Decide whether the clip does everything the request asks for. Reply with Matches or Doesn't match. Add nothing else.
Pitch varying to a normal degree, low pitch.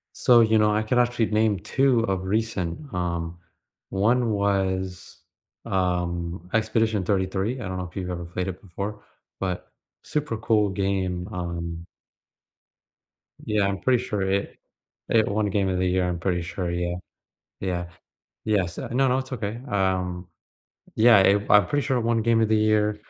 Matches